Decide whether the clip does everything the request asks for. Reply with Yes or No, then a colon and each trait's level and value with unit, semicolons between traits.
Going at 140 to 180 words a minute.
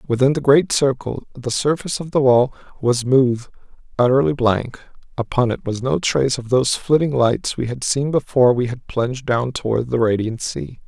No: average, 190 wpm